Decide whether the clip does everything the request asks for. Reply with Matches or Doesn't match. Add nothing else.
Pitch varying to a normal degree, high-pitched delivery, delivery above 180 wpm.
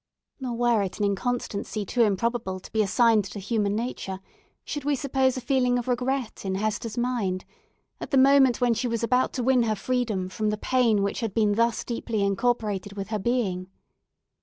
Matches